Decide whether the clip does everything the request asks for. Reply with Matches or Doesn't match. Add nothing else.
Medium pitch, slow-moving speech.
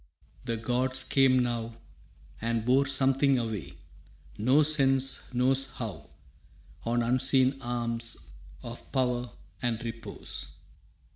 Doesn't match